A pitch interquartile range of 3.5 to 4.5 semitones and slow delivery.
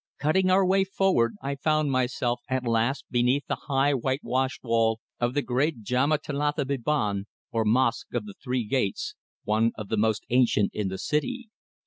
No: average, 4.0 semitones; average, 170 wpm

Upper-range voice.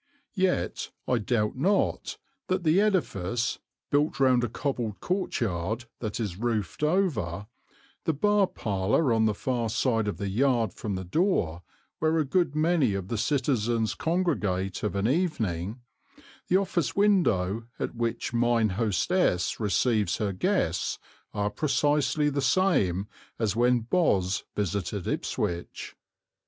No: low, 115 Hz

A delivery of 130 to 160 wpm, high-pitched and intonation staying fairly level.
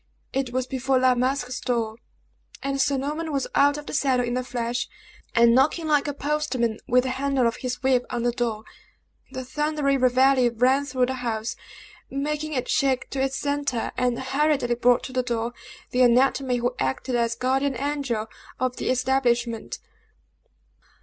No: average, 170 wpm; very high, 255 Hz; narrow, 2.2 semitones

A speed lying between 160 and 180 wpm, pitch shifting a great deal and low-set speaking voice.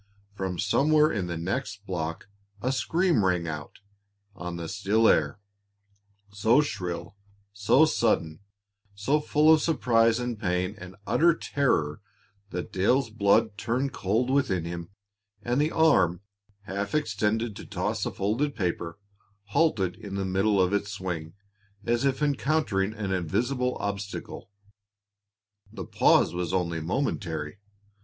No: slow, 135 wpm; wide, 5.7 semitones; low, 100 Hz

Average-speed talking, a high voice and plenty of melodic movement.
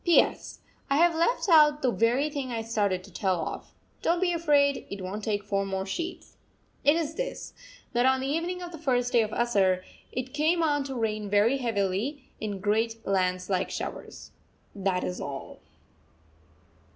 Yes: average, 175 wpm; high, 240 Hz; wide, 6.9 semitones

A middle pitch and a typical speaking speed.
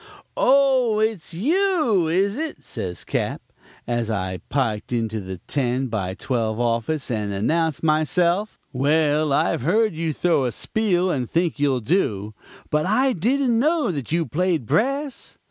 Yes: medium, 160 Hz; average, 145 wpm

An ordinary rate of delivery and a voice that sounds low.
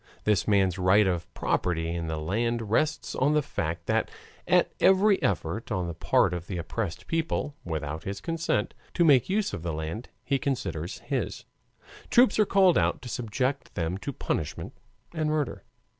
Yes: average, 175 wpm; low, 105 Hz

